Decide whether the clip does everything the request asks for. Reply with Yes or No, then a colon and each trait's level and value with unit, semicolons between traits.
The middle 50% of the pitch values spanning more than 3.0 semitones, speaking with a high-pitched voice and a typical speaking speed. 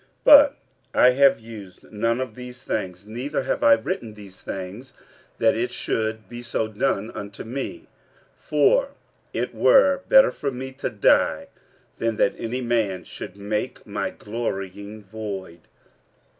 No: average, 4.3 semitones; low, 115 Hz; average, 145 wpm